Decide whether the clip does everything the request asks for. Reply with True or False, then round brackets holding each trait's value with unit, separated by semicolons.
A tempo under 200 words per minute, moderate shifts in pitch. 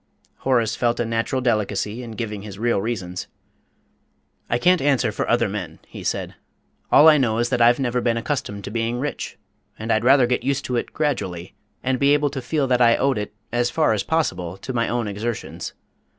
False (205 wpm; 3.3 semitones)